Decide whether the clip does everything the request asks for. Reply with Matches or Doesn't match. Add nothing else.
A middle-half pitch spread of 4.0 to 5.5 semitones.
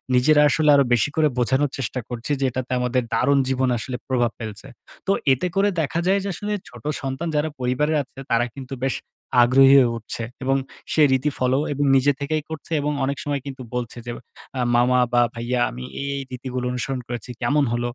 Doesn't match